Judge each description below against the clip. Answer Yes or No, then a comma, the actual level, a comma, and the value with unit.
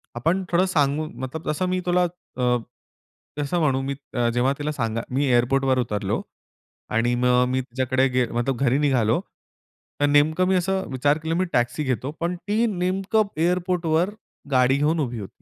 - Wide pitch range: Yes, wide, 5.7 semitones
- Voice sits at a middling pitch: Yes, medium, 145 Hz